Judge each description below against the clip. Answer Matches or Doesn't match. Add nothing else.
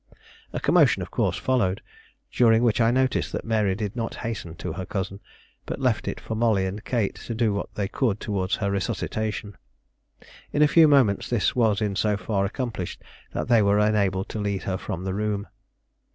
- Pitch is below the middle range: Matches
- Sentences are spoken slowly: Doesn't match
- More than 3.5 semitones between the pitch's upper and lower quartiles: Doesn't match